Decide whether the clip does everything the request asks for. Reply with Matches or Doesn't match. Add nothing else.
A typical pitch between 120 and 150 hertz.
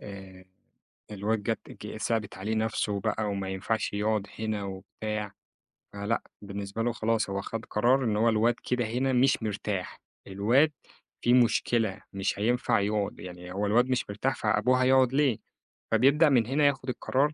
Doesn't match